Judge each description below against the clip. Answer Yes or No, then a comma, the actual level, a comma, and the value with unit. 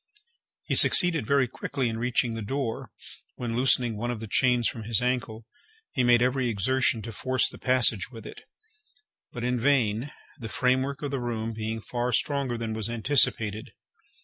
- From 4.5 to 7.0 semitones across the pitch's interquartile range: No, narrow, 2.4 semitones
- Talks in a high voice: No, low, 120 Hz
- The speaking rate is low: No, average, 175 wpm